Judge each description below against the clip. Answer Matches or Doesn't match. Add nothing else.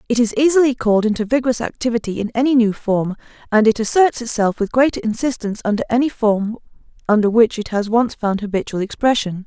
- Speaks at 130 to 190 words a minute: Matches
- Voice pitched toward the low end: Doesn't match